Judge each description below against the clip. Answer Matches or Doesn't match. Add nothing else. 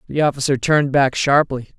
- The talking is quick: Doesn't match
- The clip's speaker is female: Matches